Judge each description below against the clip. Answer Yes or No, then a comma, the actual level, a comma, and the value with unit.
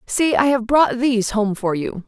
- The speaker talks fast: Yes, fast, 230 wpm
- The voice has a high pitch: Yes, high, 235 Hz